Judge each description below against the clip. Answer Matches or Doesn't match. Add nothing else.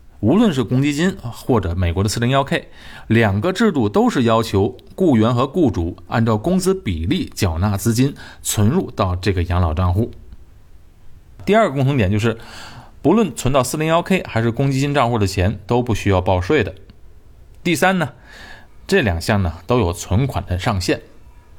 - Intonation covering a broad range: Matches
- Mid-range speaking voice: Doesn't match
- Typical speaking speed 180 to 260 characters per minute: Matches